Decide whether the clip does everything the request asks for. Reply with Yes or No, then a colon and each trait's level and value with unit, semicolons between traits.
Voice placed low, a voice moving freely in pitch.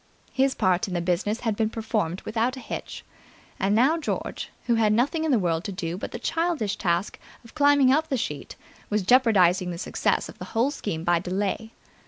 No: high, 215 Hz; wide, 5.9 semitones